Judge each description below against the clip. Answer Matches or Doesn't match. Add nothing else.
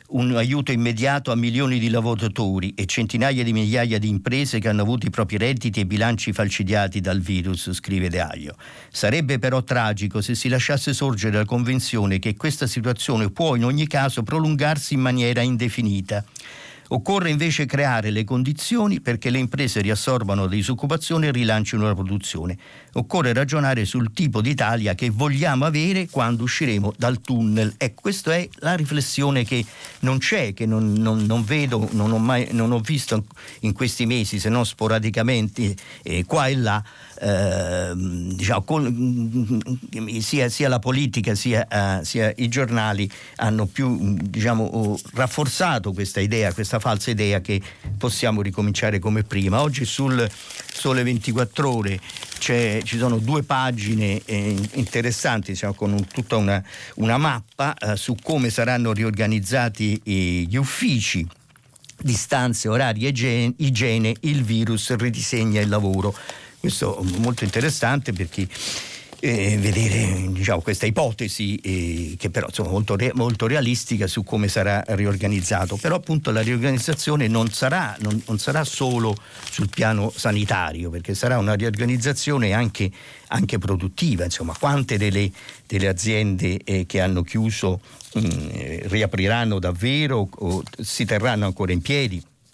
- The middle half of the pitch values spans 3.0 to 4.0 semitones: Matches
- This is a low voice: Matches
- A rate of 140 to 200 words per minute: Matches